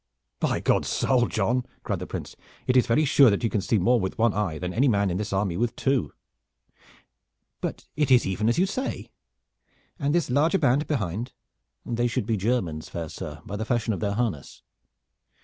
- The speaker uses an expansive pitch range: No, average, 4.6 semitones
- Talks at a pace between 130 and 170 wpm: No, average, 200 wpm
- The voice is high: No, low, 115 Hz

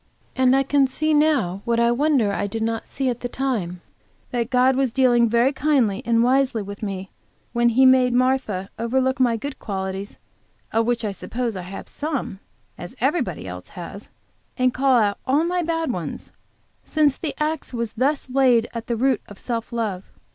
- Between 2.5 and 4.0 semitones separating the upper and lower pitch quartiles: Yes, average, 3.7 semitones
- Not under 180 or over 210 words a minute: Yes, average, 185 wpm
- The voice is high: Yes, high, 245 Hz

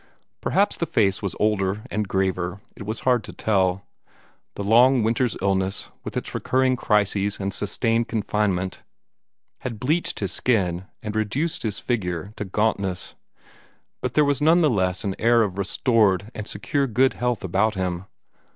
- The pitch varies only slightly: No, average, 3.7 semitones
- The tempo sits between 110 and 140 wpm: No, average, 160 wpm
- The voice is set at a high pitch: No, low, 105 Hz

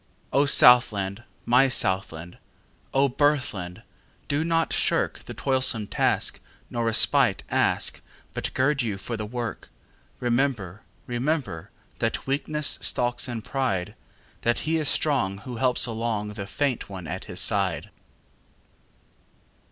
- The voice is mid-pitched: No, low, 120 Hz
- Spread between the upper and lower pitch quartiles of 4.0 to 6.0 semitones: Yes, average, 4.9 semitones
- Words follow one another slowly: Yes, slow, 105 wpm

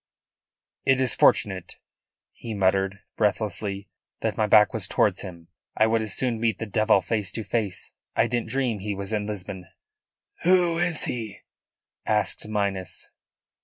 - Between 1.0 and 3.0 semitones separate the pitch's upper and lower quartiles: Yes, average, 2.7 semitones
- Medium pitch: No, low, 105 Hz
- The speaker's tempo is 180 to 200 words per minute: No, average, 150 wpm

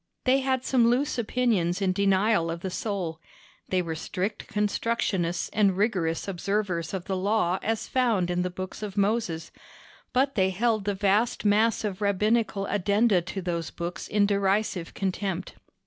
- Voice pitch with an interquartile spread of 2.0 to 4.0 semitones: Yes, average, 3.1 semitones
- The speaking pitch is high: Yes, high, 200 Hz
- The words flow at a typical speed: Yes, average, 160 wpm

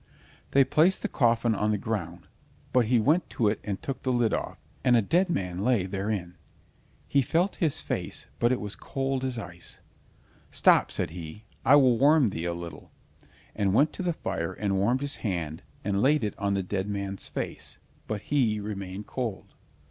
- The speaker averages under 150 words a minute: No, average, 190 wpm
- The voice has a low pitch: Yes, low, 110 Hz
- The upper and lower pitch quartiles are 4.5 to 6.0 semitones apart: Yes, average, 5.3 semitones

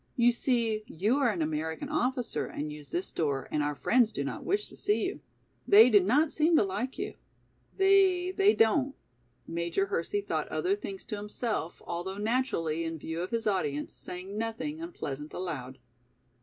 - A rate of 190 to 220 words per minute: No, average, 170 wpm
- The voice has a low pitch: No, high, 215 Hz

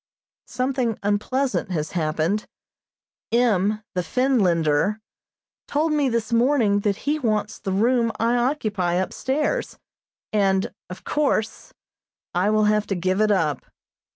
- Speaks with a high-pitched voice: Yes, high, 215 Hz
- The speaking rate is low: Yes, slow, 125 wpm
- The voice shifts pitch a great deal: No, average, 4.7 semitones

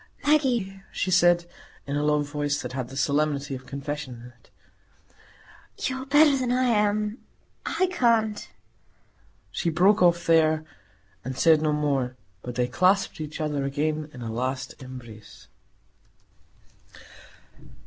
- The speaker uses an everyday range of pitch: No, wide, 7.0 semitones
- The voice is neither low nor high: Yes, medium, 155 Hz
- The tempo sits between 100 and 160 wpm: Yes, average, 140 wpm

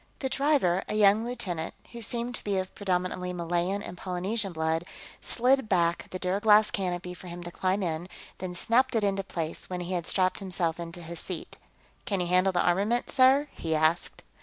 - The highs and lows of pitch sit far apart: No, average, 3.2 semitones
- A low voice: No, medium, 185 Hz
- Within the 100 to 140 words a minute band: No, average, 190 wpm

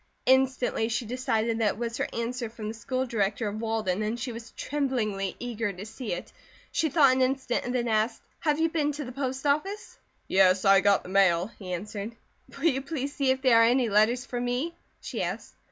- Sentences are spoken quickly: Yes, fast, 215 wpm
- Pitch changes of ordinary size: Yes, average, 3.6 semitones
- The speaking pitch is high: Yes, high, 235 Hz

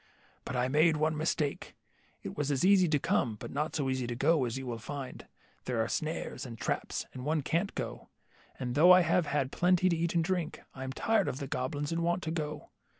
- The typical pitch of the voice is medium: Yes, medium, 150 Hz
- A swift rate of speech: Yes, fast, 225 wpm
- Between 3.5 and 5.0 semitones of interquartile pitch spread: Yes, average, 4.2 semitones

